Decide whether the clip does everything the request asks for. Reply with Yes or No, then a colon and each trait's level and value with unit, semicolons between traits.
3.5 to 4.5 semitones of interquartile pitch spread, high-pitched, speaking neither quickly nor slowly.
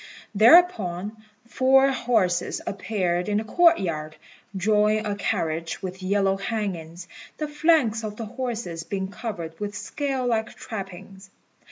No: average, 4.2 semitones; high, 205 Hz; slow, 130 wpm